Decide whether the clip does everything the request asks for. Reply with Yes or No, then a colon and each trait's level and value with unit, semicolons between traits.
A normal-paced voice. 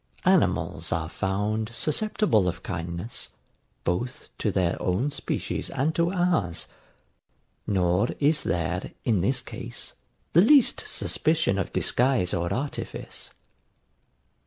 No: slow, 110 wpm